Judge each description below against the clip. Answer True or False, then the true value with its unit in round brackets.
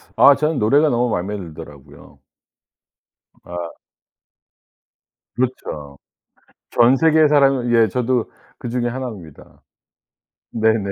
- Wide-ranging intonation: True (6.8 semitones)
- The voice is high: False (115 Hz)